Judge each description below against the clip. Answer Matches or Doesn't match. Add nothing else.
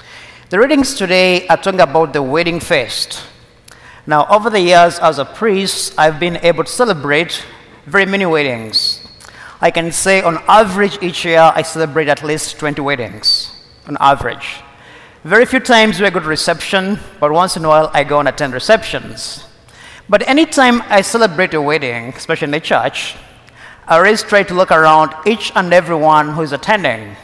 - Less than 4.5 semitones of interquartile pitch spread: Doesn't match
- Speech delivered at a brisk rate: Doesn't match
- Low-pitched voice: Doesn't match